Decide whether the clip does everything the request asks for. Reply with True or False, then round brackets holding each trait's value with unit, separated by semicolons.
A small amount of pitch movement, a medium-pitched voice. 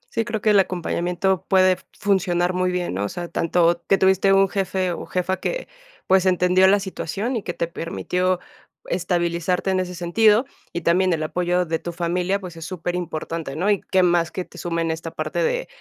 True (1.8 semitones; 180 Hz)